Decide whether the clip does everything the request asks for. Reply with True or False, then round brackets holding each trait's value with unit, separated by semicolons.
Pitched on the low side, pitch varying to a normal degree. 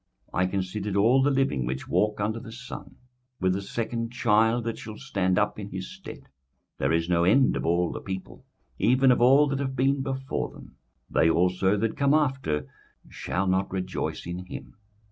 False (105 Hz; 5.8 semitones)